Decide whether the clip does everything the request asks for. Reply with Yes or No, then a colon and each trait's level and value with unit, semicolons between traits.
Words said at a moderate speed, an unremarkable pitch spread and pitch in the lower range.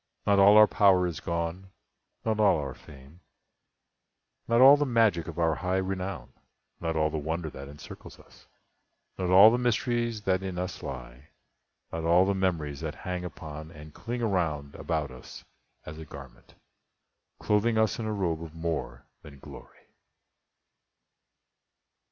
Yes: average, 150 wpm; average, 4.6 semitones; very low, 90 Hz